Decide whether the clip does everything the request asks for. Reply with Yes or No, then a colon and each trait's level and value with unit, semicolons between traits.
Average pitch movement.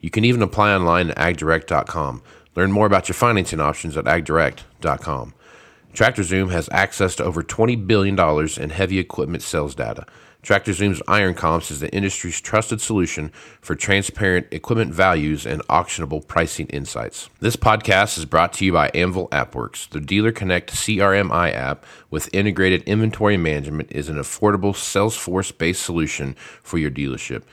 Yes: average, 4.4 semitones